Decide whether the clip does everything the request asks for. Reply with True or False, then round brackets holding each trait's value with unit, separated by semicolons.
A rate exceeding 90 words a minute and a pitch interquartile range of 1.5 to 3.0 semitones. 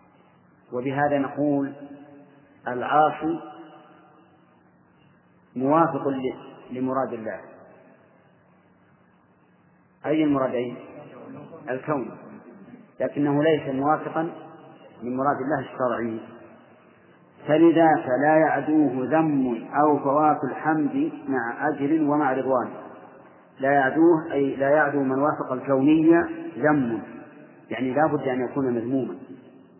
False (85 wpm; 2.7 semitones)